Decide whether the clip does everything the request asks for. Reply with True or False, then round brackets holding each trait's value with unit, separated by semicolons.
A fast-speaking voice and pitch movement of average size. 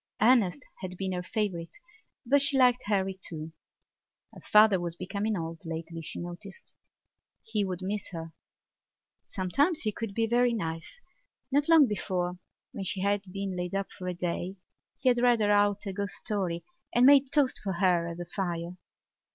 False (175 wpm; 4.2 semitones)